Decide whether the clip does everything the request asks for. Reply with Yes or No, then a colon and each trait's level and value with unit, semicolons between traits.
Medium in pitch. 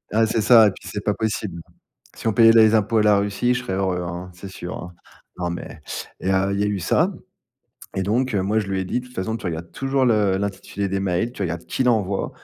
No: low, 100 Hz